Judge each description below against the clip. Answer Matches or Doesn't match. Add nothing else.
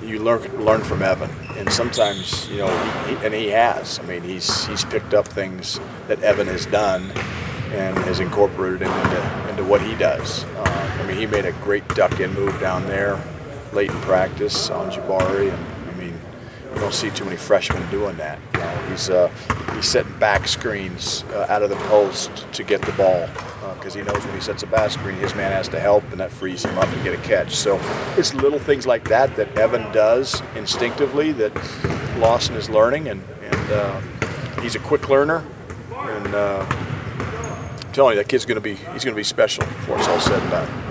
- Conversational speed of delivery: Doesn't match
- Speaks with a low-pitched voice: Matches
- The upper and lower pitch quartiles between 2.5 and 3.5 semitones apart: Doesn't match